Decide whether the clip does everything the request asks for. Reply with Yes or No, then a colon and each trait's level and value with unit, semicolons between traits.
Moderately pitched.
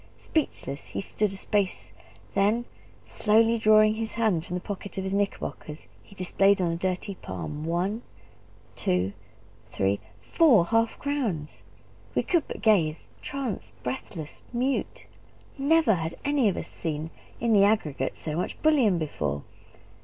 No: high, 200 Hz